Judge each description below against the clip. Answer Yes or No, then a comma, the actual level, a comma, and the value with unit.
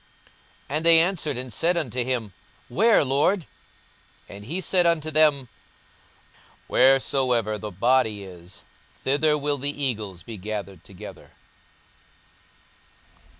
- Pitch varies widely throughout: Yes, wide, 6.4 semitones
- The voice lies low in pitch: Yes, low, 130 Hz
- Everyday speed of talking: No, slow, 115 wpm